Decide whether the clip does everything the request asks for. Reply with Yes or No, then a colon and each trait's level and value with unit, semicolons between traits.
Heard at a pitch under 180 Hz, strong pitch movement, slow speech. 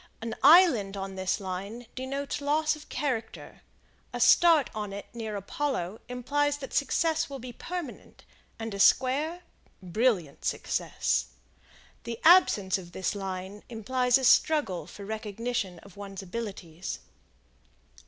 No: high, 230 Hz; wide, 6.2 semitones; slow, 130 wpm